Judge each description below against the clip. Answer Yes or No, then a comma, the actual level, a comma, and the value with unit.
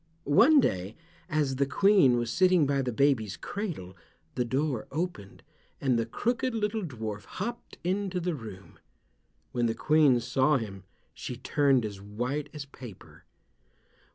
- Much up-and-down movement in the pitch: Yes, wide, 7.4 semitones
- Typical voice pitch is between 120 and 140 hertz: Yes, low, 135 Hz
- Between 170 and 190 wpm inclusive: No, average, 145 wpm